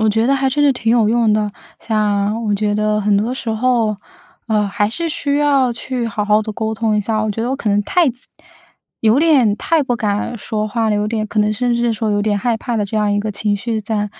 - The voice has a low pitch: No, high, 220 Hz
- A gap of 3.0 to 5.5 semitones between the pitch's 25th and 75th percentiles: No, narrow, 2.4 semitones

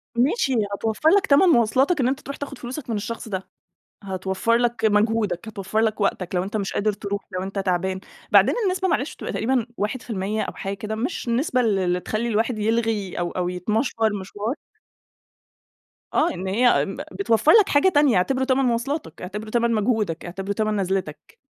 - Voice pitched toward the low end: No, high, 220 Hz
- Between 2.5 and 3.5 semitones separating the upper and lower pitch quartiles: No, average, 4.1 semitones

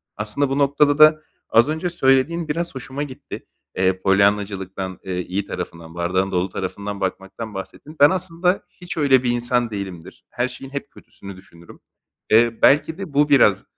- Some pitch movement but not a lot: No, wide, 7.1 semitones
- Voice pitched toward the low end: Yes, low, 120 Hz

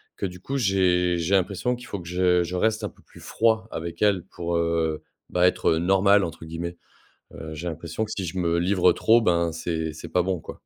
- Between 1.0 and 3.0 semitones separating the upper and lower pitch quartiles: Yes, narrow, 2.6 semitones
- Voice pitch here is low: Yes, very low, 90 Hz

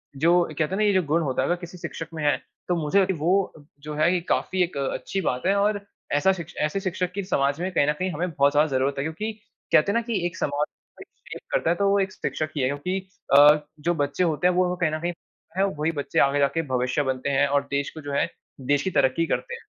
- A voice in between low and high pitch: Yes, medium, 165 Hz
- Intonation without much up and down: No, average, 4.3 semitones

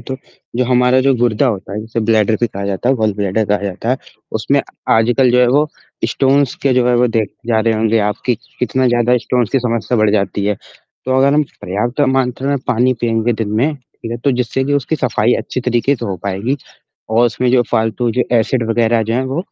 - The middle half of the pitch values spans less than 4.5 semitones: Yes, narrow, 2.5 semitones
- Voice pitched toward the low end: Yes, low, 120 Hz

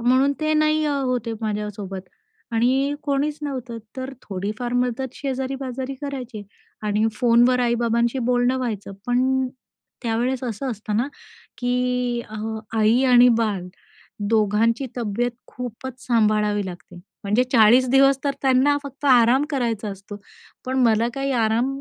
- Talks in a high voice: Yes, high, 245 Hz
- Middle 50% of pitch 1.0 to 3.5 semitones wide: Yes, average, 3.0 semitones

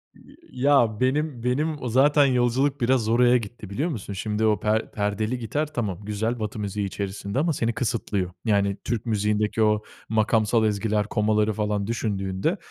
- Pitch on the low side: Yes, low, 110 Hz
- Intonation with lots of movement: No, average, 3.1 semitones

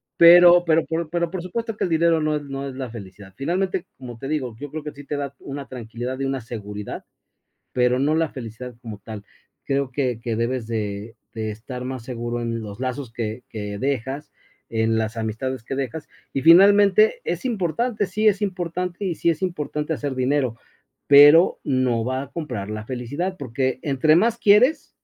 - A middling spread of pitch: No, wide, 6.1 semitones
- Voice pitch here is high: No, low, 135 Hz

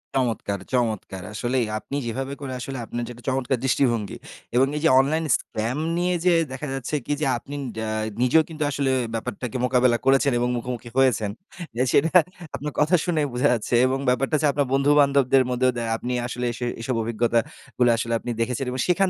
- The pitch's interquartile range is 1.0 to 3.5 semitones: Yes, average, 2.7 semitones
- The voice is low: Yes, low, 125 Hz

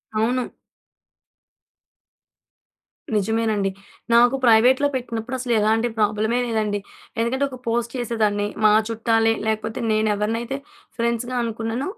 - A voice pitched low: No, high, 225 Hz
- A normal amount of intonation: No, narrow, 1.8 semitones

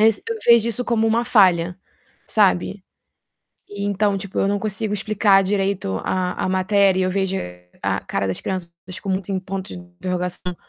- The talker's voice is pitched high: Yes, high, 195 Hz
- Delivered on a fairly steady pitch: Yes, narrow, 2.0 semitones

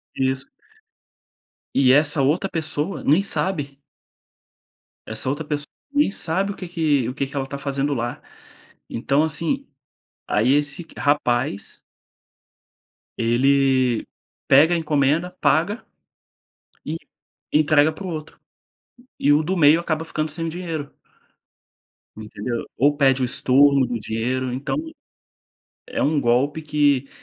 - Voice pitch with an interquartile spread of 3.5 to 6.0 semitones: No, average, 3.1 semitones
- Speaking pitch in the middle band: Yes, medium, 145 Hz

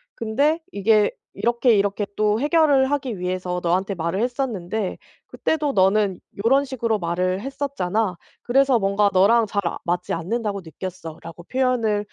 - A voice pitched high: Yes, high, 210 Hz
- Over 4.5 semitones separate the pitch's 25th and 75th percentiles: Yes, average, 5.3 semitones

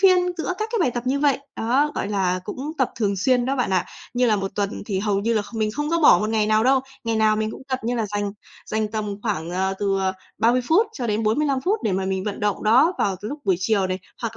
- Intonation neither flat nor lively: Yes, average, 4.4 semitones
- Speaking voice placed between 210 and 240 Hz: Yes, high, 220 Hz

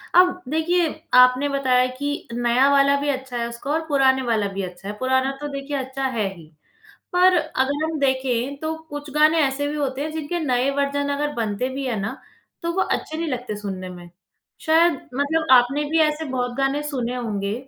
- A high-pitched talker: Yes, very high, 270 Hz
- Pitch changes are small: No, average, 3.2 semitones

